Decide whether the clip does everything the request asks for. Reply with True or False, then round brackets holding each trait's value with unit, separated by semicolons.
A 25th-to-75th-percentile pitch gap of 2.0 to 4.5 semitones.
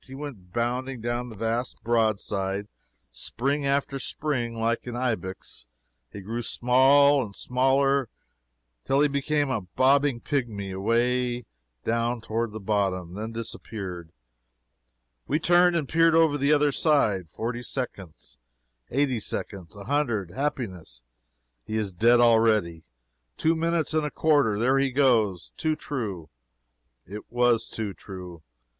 False (5.0 semitones)